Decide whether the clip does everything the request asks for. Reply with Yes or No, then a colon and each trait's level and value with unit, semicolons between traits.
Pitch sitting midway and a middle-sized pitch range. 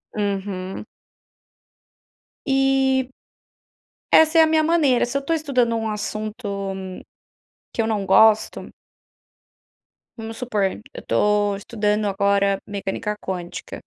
No: high, 215 Hz; average, 4.6 semitones